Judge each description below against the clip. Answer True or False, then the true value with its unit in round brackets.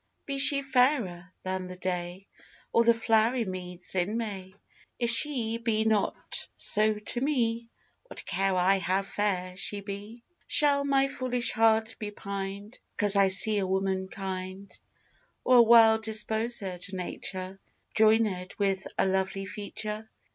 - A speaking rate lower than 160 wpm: True (140 wpm)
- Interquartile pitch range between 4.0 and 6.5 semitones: False (3.3 semitones)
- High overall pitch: True (210 Hz)